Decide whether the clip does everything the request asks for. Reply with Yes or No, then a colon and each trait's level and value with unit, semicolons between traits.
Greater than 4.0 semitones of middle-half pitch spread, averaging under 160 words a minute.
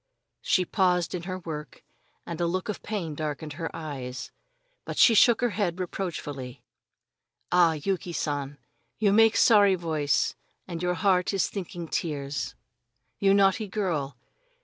Yes: average, 4.4 semitones; average, 145 wpm